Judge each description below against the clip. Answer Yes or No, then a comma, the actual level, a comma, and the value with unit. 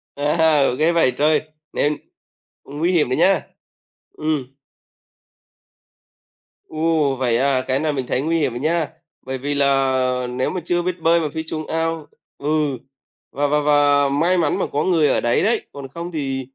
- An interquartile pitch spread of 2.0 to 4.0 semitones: Yes, average, 3.1 semitones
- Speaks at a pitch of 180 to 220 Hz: No, medium, 150 Hz